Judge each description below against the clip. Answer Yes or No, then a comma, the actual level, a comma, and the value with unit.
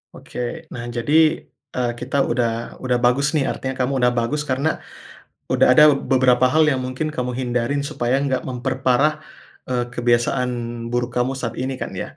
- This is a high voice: No, low, 125 Hz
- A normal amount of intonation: No, narrow, 2.1 semitones